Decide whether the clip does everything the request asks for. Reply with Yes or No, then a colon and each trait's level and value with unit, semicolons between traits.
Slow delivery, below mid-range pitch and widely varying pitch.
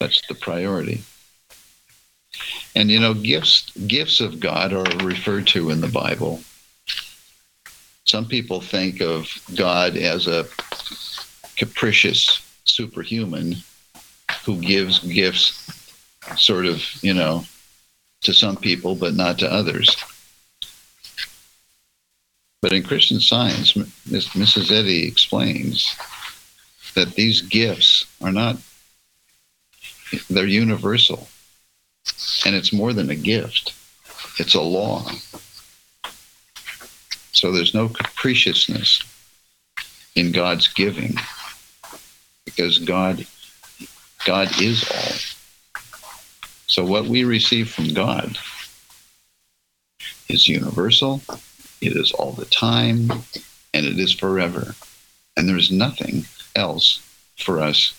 No: slow, 100 wpm; very low, 95 Hz; average, 4.2 semitones